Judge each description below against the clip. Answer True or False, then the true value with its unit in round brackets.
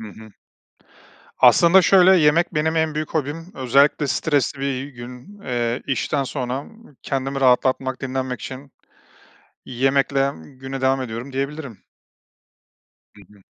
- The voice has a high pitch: False (135 Hz)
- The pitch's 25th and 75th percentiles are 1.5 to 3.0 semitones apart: True (2.6 semitones)